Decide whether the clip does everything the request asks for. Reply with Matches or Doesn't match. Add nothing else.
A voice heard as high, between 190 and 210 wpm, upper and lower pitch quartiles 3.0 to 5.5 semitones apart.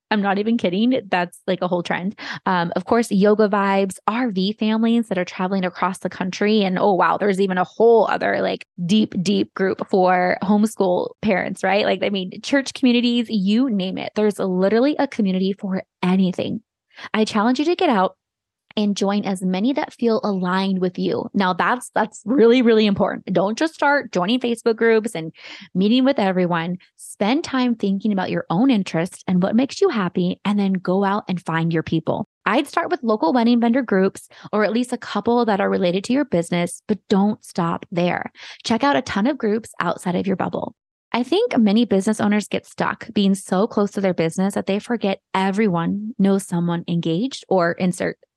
Matches